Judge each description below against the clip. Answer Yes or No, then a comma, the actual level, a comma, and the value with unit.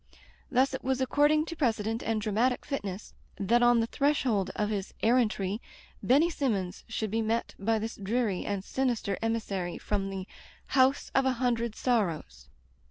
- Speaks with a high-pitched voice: Yes, high, 225 Hz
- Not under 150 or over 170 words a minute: Yes, average, 160 wpm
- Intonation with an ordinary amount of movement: Yes, average, 4.1 semitones